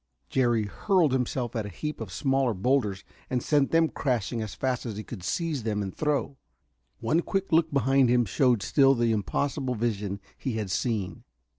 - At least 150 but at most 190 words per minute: Yes, average, 180 wpm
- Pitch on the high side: No, low, 125 Hz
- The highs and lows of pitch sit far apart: No, average, 4.4 semitones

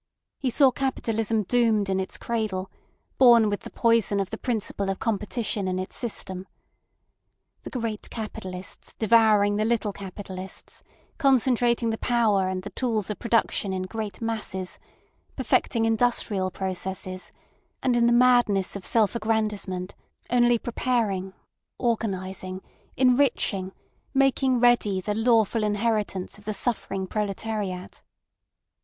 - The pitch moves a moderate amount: Yes, average, 3.6 semitones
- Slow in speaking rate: Yes, slow, 125 wpm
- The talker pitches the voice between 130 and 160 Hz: No, high, 215 Hz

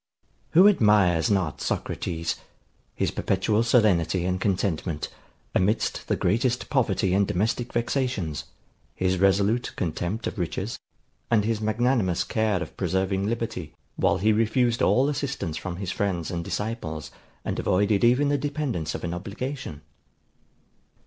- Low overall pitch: Yes, low, 100 Hz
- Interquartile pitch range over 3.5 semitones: Yes, average, 4.7 semitones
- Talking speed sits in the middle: No, slow, 130 wpm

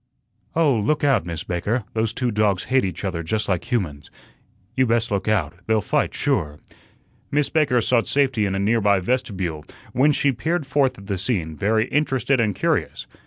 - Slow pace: No, average, 180 wpm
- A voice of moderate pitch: No, low, 110 Hz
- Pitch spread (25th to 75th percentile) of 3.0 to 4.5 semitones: No, wide, 5.4 semitones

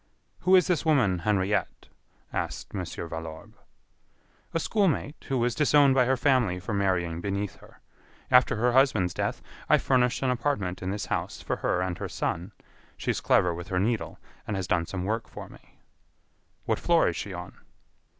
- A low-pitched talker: Yes, low, 105 Hz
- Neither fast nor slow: Yes, average, 180 wpm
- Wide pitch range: Yes, wide, 6.4 semitones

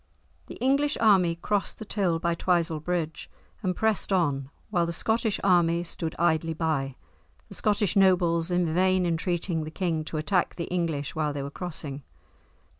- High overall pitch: No, medium, 170 Hz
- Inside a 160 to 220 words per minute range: Yes, average, 165 wpm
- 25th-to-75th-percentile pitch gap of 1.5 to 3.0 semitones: Yes, average, 2.7 semitones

